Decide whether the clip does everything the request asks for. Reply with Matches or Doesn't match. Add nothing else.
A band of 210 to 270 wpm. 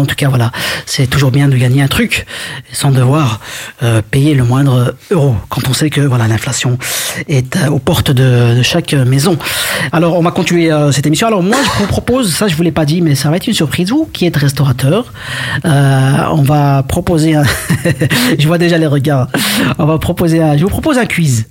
Matches